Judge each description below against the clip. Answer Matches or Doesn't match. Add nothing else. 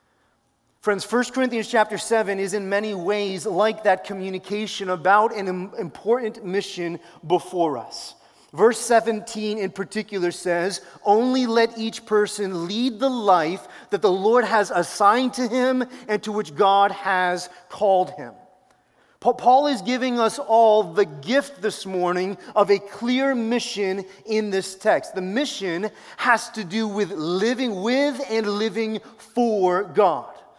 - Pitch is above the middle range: Matches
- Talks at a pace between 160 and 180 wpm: Doesn't match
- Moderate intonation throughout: Matches